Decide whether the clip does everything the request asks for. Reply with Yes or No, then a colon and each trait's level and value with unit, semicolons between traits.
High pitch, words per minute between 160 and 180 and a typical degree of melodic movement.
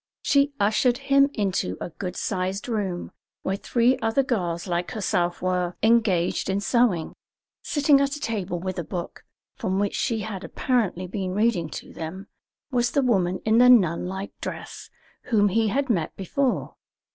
Yes: high, 200 Hz; average, 165 wpm; average, 4.9 semitones